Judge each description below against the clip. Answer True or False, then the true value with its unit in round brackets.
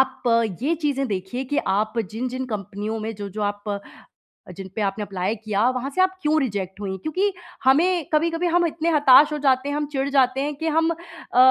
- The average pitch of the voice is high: True (260 Hz)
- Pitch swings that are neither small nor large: False (6.4 semitones)